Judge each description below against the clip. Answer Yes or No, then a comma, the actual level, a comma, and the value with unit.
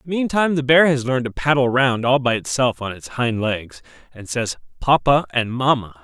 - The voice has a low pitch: Yes, low, 130 Hz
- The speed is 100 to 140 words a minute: No, average, 200 wpm